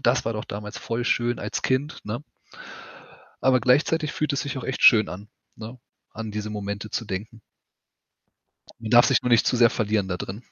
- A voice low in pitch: Yes, low, 115 Hz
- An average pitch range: Yes, average, 3.2 semitones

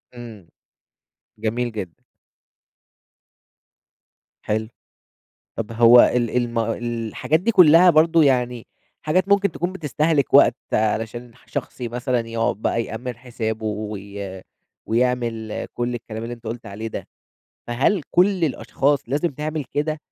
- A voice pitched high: No, low, 120 Hz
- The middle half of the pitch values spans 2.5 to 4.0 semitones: No, average, 5.0 semitones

